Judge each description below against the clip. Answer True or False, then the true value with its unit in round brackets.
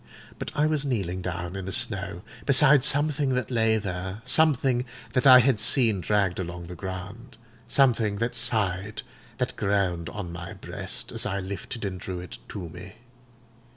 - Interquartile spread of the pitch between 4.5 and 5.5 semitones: True (5.1 semitones)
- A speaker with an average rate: True (155 wpm)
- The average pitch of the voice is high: False (105 Hz)